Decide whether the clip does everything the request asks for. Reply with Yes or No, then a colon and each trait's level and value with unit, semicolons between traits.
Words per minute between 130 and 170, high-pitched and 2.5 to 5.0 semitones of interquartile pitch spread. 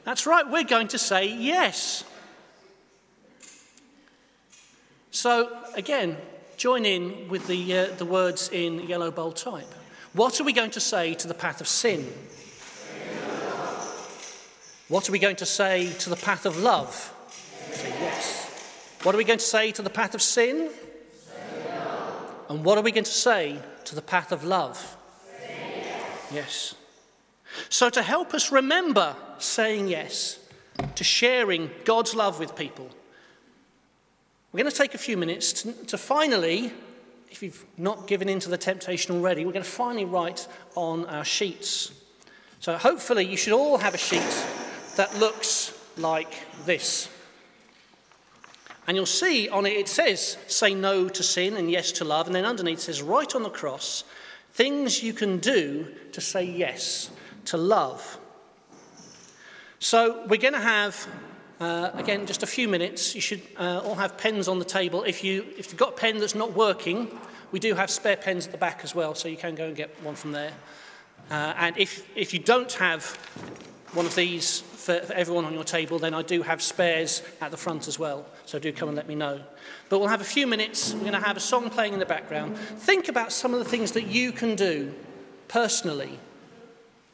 No: average, 180 wpm; high, 195 Hz; average, 4.6 semitones